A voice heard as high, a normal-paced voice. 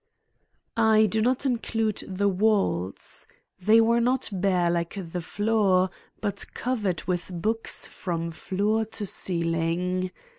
No: high, 200 Hz; slow, 120 wpm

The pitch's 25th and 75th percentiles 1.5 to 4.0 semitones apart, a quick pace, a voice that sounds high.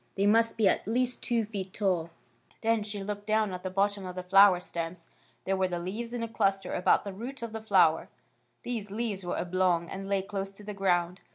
Yes: average, 2.9 semitones; fast, 225 wpm; high, 195 Hz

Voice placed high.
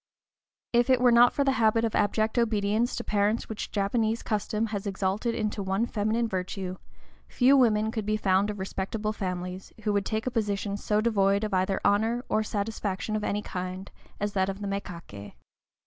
Yes: high, 210 Hz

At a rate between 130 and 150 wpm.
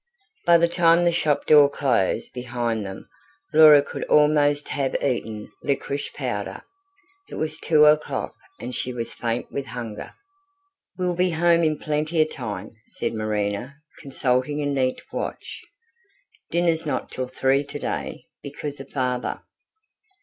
Yes: average, 140 wpm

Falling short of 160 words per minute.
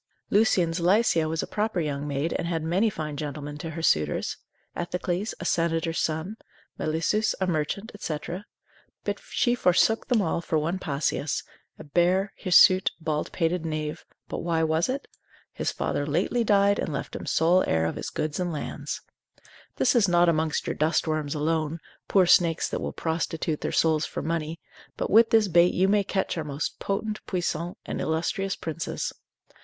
No: average, 175 wpm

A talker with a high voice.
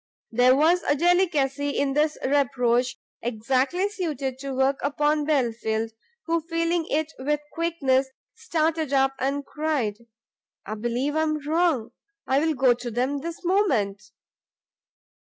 Yes: very high, 285 Hz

